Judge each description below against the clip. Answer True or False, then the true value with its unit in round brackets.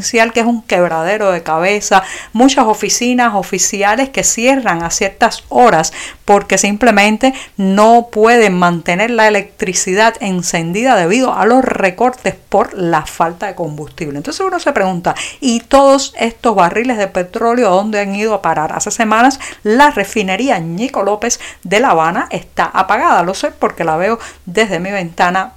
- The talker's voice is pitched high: True (205 Hz)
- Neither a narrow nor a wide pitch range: True (4.0 semitones)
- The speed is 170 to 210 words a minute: False (155 wpm)